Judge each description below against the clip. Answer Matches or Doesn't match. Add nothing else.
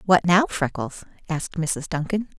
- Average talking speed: Matches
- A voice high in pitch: Doesn't match